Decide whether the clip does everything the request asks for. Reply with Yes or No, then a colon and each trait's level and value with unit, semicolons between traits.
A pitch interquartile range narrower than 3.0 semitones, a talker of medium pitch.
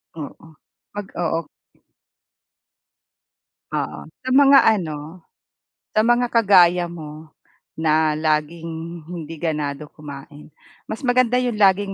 No: average, 5.0 semitones; medium, 165 Hz